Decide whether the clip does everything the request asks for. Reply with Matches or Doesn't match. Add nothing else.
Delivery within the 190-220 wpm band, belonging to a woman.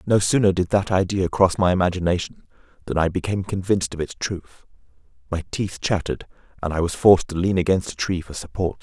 Doesn't match